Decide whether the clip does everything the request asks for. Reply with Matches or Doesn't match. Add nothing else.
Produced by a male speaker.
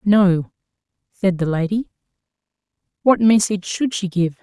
Doesn't match